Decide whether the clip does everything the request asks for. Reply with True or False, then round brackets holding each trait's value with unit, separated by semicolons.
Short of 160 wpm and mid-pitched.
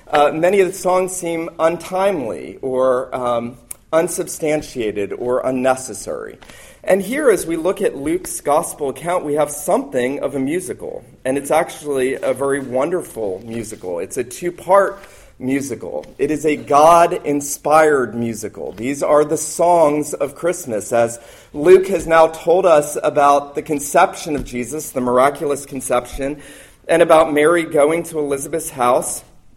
True (145 wpm; 150 Hz)